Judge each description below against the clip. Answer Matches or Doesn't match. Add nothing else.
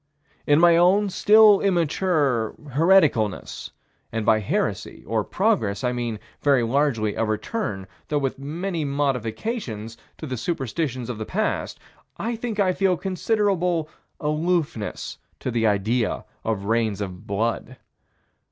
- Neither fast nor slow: Doesn't match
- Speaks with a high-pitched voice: Doesn't match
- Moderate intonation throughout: Doesn't match